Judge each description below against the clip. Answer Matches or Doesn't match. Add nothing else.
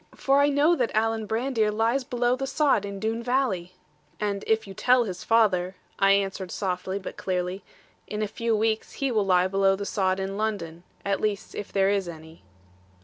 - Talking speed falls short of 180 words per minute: Doesn't match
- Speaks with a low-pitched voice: Doesn't match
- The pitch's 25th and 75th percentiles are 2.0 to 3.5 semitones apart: Matches